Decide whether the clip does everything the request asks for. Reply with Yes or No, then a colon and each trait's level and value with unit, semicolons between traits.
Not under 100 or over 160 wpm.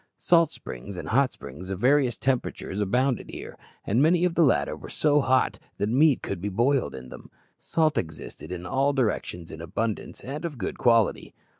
No: average, 185 wpm